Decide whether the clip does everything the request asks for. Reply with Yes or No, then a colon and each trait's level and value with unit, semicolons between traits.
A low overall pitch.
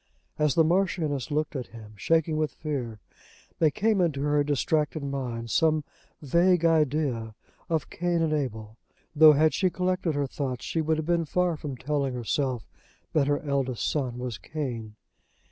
No: medium, 150 Hz